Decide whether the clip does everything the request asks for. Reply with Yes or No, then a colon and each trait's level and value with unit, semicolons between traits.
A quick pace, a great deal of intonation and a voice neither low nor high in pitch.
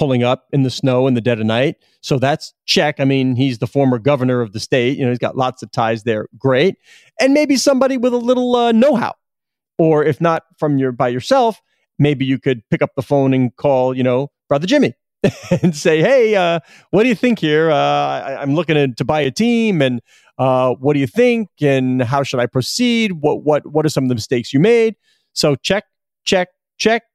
Yes: fast, 225 wpm; wide, 6.7 semitones; medium, 145 Hz